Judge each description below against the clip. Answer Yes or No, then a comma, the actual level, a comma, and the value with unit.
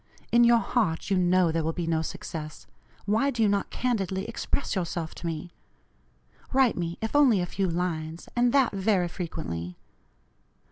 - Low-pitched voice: No, medium, 185 Hz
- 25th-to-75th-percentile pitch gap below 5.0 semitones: No, wide, 5.5 semitones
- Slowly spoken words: No, average, 170 wpm